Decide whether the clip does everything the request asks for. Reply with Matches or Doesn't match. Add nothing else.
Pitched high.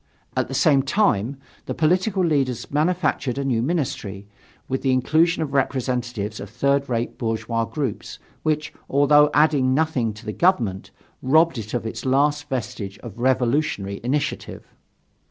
Doesn't match